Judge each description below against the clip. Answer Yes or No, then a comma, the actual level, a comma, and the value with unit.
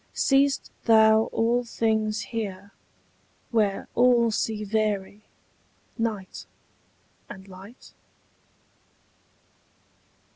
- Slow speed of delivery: Yes, slow, 70 wpm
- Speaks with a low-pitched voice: No, high, 220 Hz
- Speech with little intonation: Yes, narrow, 2.2 semitones